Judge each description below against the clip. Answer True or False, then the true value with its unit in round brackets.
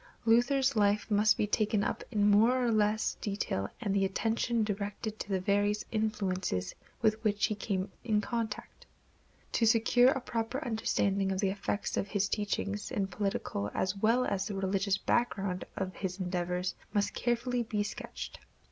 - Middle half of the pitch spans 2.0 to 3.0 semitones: True (2.5 semitones)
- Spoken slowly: False (165 wpm)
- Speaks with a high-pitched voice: True (210 Hz)